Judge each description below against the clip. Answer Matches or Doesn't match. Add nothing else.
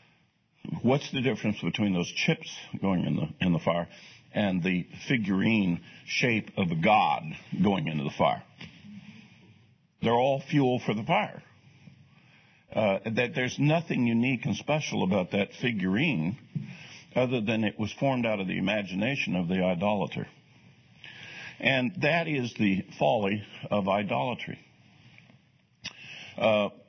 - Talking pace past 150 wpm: Doesn't match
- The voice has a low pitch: Matches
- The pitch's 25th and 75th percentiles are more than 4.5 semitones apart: Matches